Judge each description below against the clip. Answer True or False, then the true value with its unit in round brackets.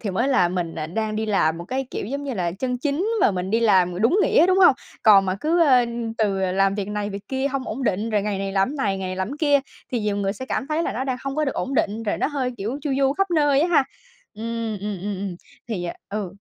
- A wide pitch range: True (5.8 semitones)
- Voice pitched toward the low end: False (220 Hz)